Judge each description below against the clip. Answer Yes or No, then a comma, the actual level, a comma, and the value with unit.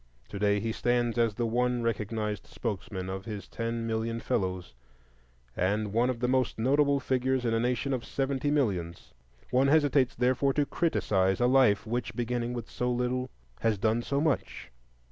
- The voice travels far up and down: No, average, 3.0 semitones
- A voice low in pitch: Yes, low, 120 Hz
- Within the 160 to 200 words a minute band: Yes, average, 170 wpm